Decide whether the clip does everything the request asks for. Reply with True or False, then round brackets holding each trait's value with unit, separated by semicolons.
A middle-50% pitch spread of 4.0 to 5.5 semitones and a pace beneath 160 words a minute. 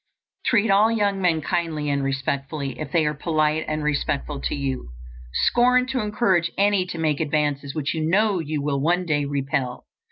False (4.7 semitones; 180 wpm)